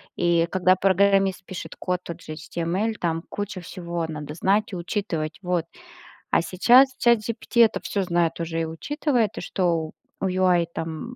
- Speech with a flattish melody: No, average, 3.2 semitones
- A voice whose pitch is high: No, medium, 180 Hz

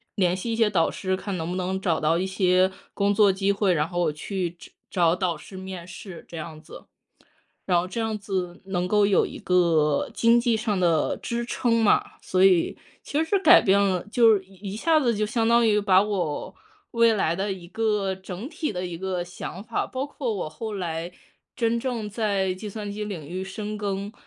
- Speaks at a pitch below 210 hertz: Yes, high, 195 Hz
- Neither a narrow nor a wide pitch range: Yes, average, 3.3 semitones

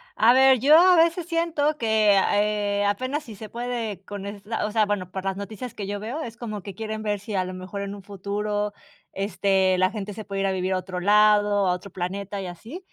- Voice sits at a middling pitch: No, high, 205 Hz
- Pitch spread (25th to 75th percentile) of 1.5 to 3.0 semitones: Yes, narrow, 2.5 semitones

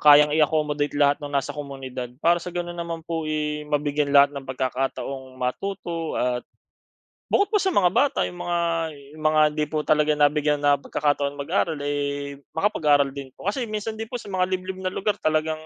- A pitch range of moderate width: Yes, average, 3.4 semitones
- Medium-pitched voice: Yes, medium, 150 Hz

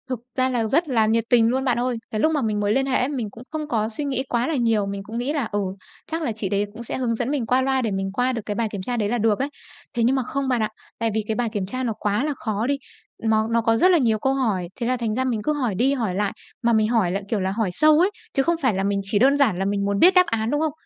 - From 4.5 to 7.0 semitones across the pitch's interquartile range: No, average, 3.7 semitones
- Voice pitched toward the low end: No, high, 235 Hz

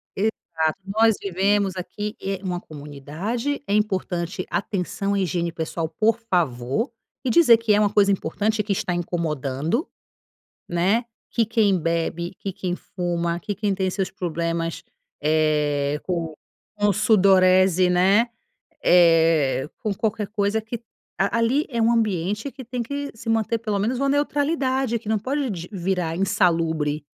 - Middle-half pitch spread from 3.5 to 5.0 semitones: Yes, average, 4.7 semitones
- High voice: Yes, high, 195 Hz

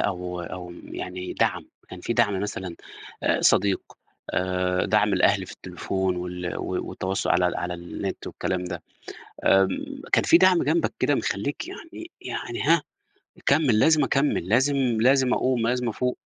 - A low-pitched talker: Yes, low, 100 Hz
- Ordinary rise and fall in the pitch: No, wide, 6.4 semitones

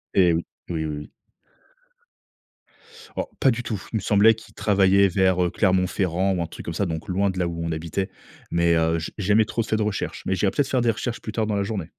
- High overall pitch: No, very low, 95 Hz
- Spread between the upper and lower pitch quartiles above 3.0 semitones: Yes, average, 3.8 semitones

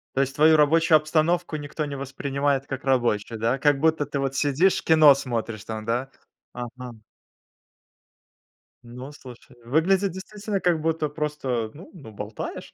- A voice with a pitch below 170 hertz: Yes, medium, 140 Hz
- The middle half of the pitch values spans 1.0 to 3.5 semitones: No, average, 4.1 semitones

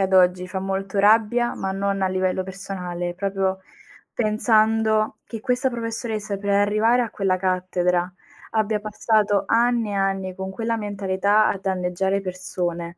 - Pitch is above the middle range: Yes, high, 195 Hz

